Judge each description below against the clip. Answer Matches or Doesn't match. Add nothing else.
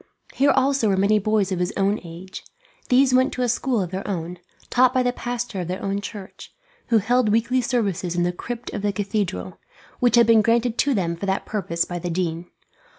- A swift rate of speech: Matches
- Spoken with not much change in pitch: Doesn't match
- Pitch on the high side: Matches